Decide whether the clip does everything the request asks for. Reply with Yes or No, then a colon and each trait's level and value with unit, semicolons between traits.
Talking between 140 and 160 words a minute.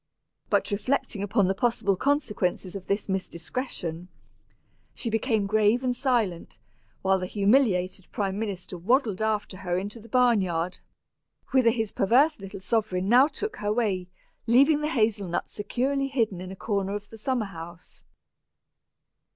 Yes: average, 150 wpm